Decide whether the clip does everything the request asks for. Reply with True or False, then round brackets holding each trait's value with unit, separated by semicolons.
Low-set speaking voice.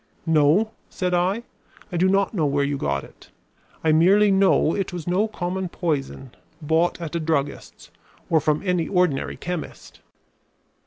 False (170 Hz)